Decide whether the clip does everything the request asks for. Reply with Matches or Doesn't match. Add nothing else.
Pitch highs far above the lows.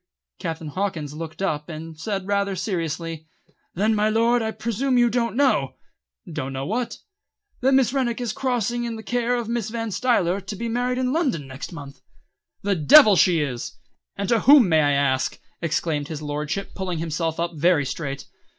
Matches